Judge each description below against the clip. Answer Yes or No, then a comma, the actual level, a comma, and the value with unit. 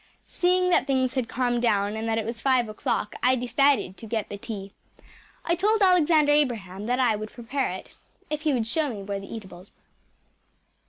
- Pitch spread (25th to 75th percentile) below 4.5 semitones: No, average, 5.2 semitones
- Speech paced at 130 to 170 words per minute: No, average, 195 wpm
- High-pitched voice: Yes, high, 240 Hz